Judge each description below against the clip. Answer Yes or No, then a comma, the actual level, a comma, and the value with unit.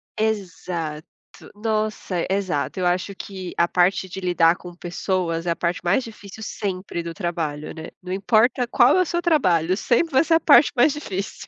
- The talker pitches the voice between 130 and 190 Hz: Yes, medium, 185 Hz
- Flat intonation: No, average, 4.1 semitones